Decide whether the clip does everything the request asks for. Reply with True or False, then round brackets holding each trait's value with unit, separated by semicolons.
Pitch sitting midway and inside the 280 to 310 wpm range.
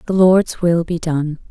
False (170 Hz; 200 wpm)